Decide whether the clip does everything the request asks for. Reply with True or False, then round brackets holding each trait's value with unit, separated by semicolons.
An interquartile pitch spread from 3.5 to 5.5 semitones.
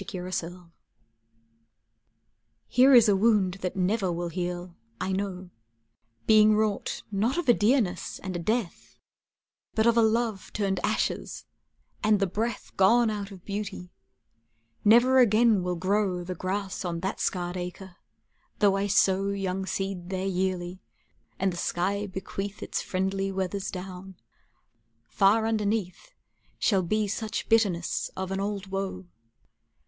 False (2.6 semitones)